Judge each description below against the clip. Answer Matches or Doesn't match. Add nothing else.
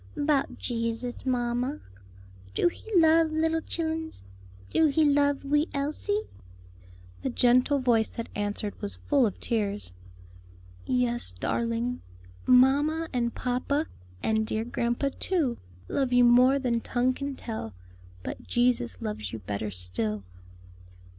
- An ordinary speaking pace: Doesn't match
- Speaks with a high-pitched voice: Matches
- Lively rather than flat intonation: Doesn't match